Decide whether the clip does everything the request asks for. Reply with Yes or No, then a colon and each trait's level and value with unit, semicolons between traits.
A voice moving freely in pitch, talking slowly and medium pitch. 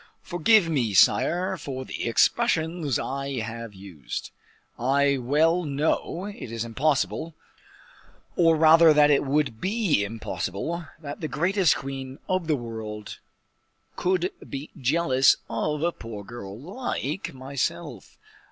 Yes: wide, 5.7 semitones; slow, 125 wpm; medium, 145 Hz